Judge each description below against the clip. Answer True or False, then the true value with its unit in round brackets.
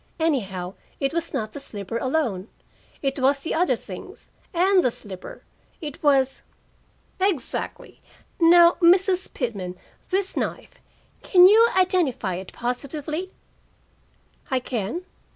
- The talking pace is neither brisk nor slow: False (120 wpm)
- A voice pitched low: False (280 Hz)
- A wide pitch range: True (7.2 semitones)